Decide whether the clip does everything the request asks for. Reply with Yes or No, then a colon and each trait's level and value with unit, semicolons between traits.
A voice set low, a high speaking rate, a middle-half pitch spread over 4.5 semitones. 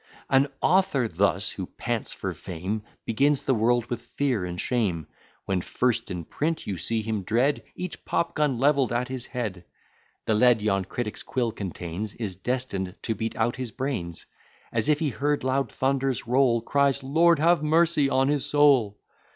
No: low, 120 Hz; average, 175 wpm; average, 4.9 semitones